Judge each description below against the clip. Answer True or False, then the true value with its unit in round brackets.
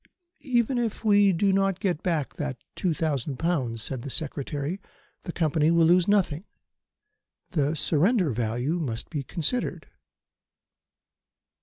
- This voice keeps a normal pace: False (130 wpm)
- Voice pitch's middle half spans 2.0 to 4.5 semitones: False (5.3 semitones)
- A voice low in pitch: False (165 Hz)